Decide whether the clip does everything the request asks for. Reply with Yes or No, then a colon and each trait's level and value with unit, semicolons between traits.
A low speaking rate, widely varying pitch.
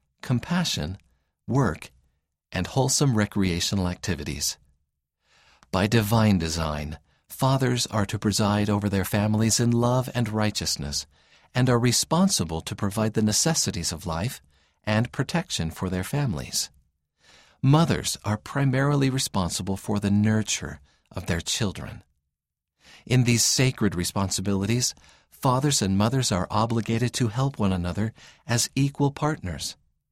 Yes: slow, 120 wpm; wide, 6.2 semitones